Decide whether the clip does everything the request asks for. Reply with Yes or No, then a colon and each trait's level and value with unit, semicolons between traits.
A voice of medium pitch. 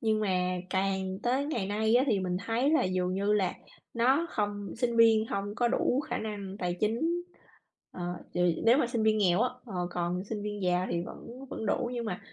No: high, 210 Hz